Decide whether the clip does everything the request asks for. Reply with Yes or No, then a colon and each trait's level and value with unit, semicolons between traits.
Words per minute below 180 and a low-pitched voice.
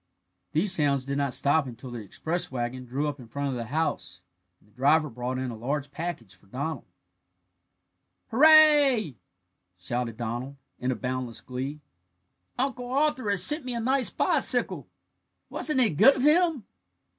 No: average, 155 wpm; medium, 145 Hz